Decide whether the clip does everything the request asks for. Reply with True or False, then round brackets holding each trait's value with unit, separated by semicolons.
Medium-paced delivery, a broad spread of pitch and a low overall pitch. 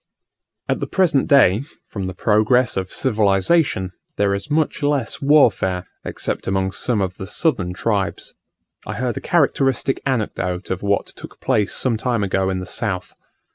True (160 wpm; 5.9 semitones; 105 Hz)